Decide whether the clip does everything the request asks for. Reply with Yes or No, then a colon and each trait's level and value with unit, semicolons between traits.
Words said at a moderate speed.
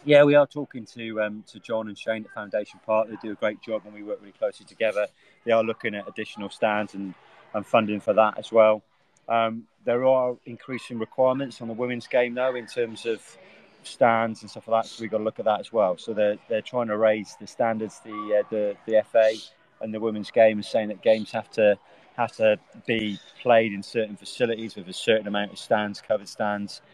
No: fast, 225 wpm